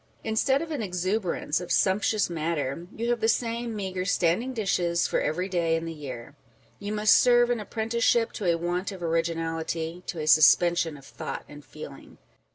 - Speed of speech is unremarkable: Yes, average, 175 wpm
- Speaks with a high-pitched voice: No, medium, 180 Hz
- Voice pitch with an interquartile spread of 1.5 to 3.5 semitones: No, average, 5.0 semitones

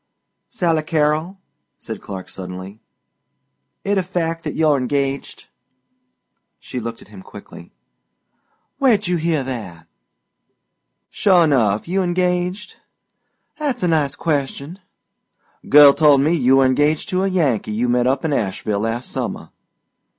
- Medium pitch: Yes, medium, 150 Hz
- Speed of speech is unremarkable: No, slow, 130 wpm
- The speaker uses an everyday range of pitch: No, wide, 6.0 semitones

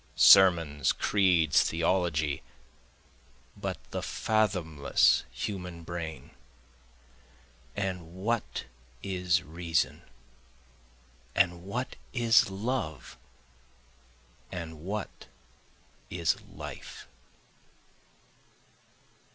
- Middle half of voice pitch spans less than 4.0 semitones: Yes, average, 3.2 semitones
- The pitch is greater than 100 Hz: No, very low, 90 Hz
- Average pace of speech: No, slow, 60 wpm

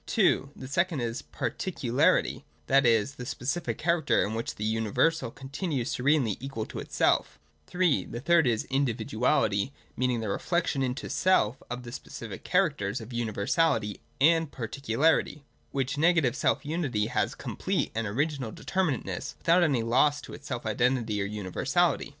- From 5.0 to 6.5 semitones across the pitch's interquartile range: Yes, wide, 5.5 semitones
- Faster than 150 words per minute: Yes, average, 160 wpm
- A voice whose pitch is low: Yes, low, 130 Hz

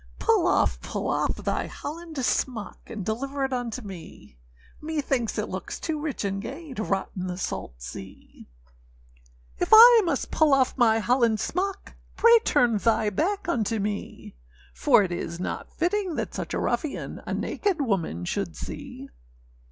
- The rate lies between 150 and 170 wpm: Yes, average, 160 wpm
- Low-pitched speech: No, very high, 250 Hz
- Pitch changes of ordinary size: No, wide, 7.7 semitones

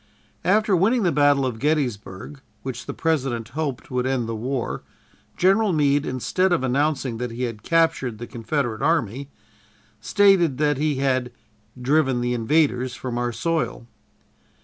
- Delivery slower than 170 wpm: Yes, average, 150 wpm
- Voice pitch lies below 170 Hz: Yes, low, 135 Hz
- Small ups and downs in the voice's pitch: No, average, 4.4 semitones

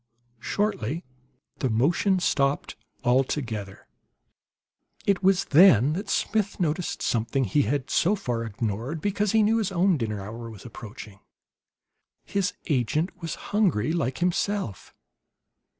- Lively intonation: Yes, wide, 8.5 semitones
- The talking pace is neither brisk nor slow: No, slow, 120 wpm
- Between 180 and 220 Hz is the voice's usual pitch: No, medium, 150 Hz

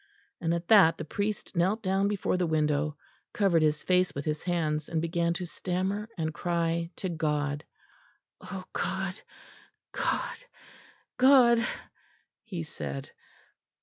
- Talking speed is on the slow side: Yes, slow, 130 wpm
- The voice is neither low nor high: Yes, medium, 170 Hz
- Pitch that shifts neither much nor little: Yes, average, 3.4 semitones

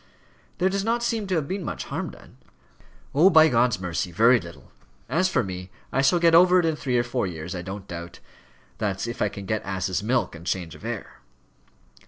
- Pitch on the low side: Yes, low, 120 Hz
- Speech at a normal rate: No, fast, 215 wpm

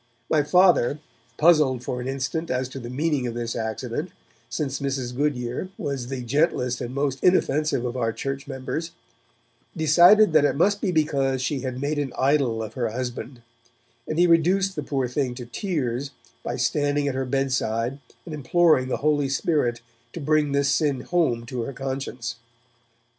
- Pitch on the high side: No, low, 135 Hz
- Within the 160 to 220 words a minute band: Yes, average, 175 wpm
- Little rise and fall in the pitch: No, average, 3.5 semitones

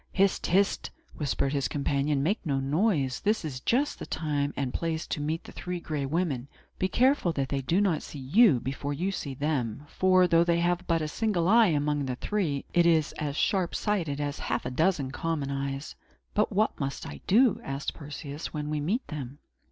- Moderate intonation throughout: Yes, average, 4.7 semitones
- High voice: No, medium, 155 Hz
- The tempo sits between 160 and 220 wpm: Yes, average, 200 wpm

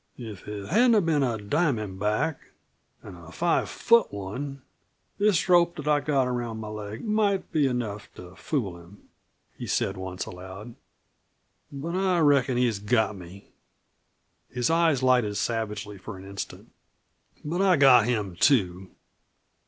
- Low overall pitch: Yes, low, 120 Hz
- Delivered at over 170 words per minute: No, average, 145 wpm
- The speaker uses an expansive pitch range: Yes, wide, 6.8 semitones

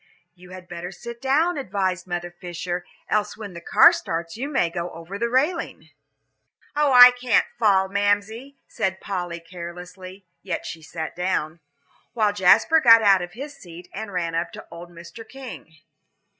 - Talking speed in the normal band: Yes, average, 165 wpm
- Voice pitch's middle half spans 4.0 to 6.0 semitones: Yes, average, 4.8 semitones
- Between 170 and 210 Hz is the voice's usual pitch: Yes, high, 190 Hz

